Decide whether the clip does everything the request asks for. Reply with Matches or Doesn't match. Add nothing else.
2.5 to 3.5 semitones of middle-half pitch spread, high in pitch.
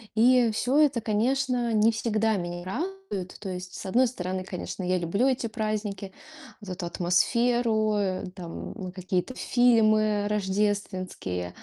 Doesn't match